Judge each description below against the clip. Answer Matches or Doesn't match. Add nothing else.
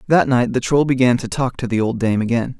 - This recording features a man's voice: Matches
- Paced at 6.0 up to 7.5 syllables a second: Doesn't match